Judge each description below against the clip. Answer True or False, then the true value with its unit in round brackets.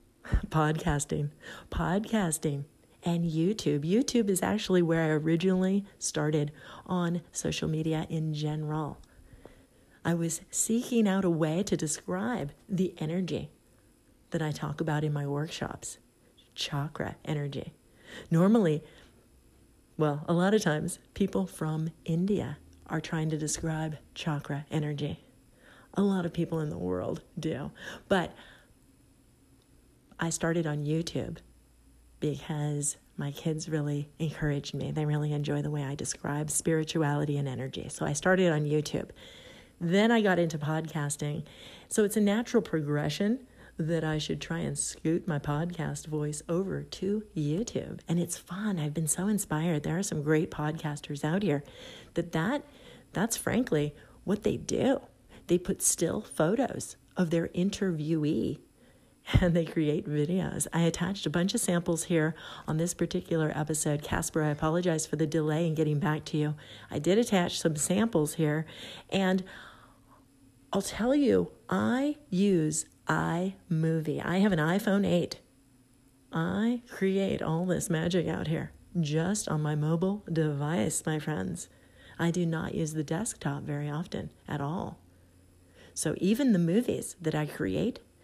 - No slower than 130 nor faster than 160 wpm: True (140 wpm)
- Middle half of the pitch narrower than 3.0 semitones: False (3.3 semitones)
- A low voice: False (160 Hz)